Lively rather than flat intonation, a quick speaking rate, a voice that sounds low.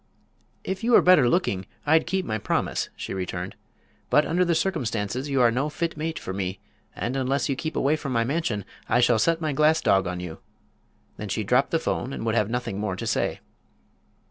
Yes: wide, 7.1 semitones; fast, 210 wpm; low, 130 Hz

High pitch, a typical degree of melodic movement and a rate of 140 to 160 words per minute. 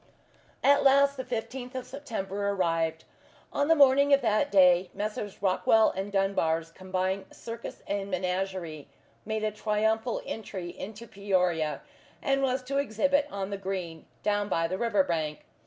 Yes: high, 200 Hz; average, 4.7 semitones; average, 150 wpm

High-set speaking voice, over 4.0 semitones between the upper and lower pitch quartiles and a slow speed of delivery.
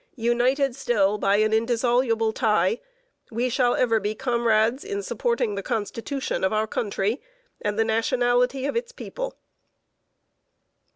No: high, 235 Hz; average, 3.0 semitones; slow, 130 wpm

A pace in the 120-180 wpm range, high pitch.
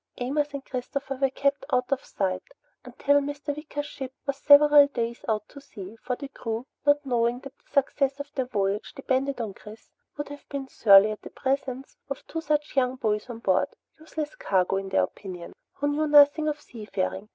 No: average, 195 wpm; very high, 270 Hz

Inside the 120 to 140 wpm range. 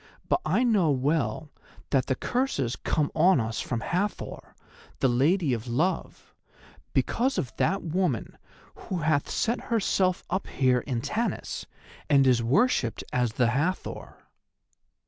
Yes: slow, 135 wpm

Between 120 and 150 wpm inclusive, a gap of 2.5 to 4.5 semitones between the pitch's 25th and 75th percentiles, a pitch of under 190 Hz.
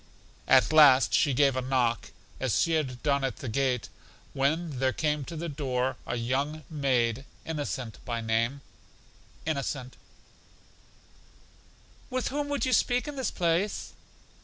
Yes: average, 140 wpm; average, 3.9 semitones; medium, 140 Hz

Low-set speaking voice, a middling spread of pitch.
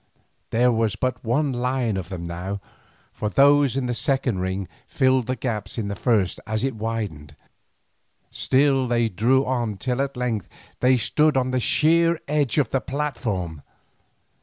Yes: low, 125 Hz; average, 4.0 semitones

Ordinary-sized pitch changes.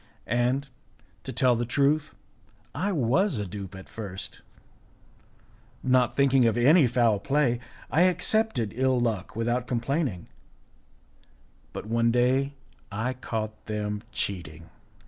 Yes: average, 4.0 semitones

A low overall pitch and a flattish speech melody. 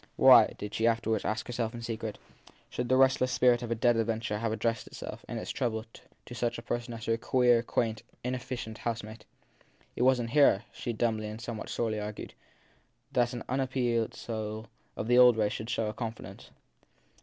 Yes: low, 115 Hz; narrow, 1.7 semitones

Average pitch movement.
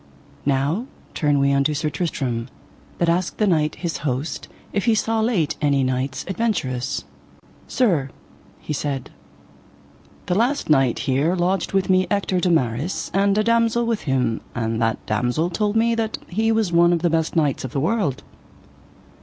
No: wide, 6.8 semitones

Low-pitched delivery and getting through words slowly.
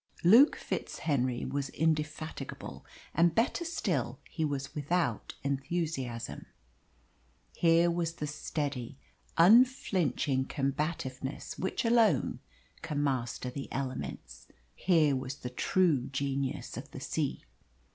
No: medium, 145 Hz; slow, 105 wpm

